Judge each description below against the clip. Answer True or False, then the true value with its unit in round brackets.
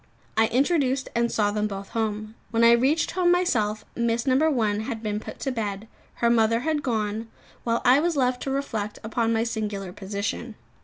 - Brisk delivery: False (190 wpm)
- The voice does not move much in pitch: False (3.4 semitones)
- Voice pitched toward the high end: True (230 Hz)